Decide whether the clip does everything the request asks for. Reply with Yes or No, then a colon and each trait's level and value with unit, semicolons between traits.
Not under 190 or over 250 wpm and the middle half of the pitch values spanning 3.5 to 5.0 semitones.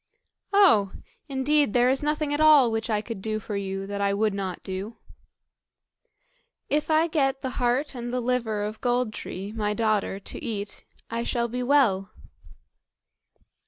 No: average, 160 wpm; average, 4.5 semitones